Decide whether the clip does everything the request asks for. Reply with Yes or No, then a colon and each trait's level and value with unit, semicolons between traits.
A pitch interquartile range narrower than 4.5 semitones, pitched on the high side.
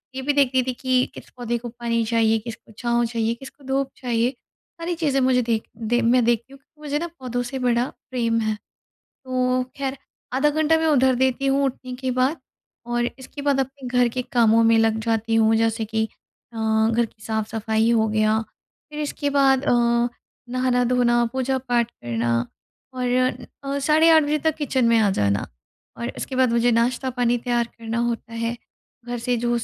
Yes: narrow, 2.5 semitones; high, 245 Hz